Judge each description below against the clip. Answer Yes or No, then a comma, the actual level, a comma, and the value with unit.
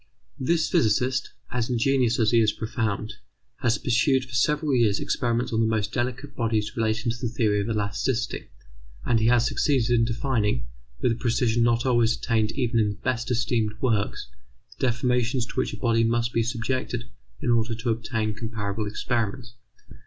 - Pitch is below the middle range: Yes, low, 115 Hz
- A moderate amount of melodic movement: No, narrow, 1.8 semitones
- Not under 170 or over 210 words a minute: Yes, average, 175 wpm